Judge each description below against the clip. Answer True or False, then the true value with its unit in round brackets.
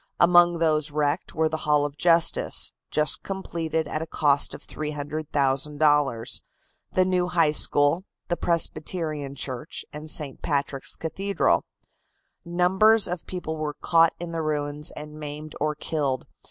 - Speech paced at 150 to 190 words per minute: False (140 wpm)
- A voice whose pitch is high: False (155 Hz)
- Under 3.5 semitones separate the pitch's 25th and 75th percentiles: True (2.4 semitones)